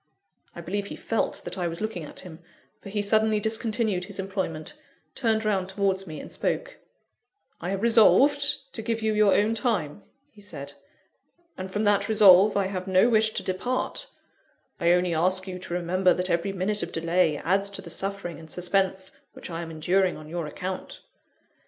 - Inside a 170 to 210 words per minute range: Yes, average, 185 wpm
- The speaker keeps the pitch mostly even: No, average, 3.1 semitones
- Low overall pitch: No, high, 195 Hz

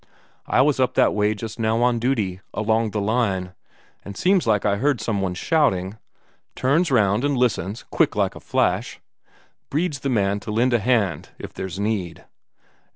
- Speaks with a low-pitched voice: Yes, low, 110 Hz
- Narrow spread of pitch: No, average, 4.1 semitones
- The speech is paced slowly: No, average, 175 wpm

